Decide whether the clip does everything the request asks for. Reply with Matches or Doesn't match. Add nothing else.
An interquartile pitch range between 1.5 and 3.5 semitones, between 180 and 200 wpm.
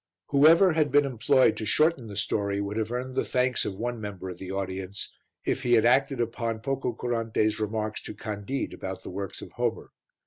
Doesn't match